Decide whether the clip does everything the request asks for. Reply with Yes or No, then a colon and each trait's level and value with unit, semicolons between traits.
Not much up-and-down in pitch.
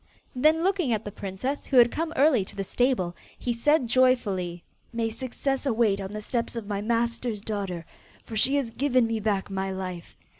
No: average, 4.4 semitones